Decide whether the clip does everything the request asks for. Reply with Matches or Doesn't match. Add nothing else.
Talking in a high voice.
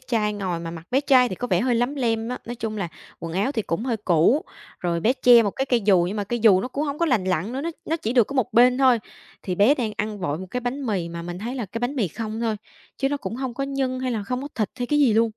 Matches